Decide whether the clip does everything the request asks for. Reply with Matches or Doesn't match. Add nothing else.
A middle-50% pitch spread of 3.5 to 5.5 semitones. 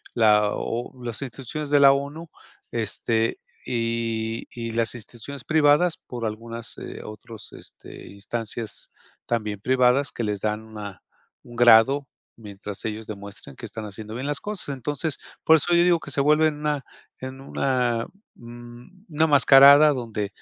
Matches